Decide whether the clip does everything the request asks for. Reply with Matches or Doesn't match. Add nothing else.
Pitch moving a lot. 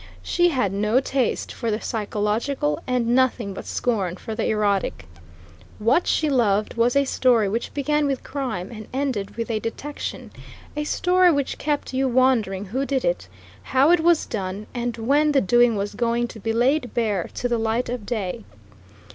Doesn't match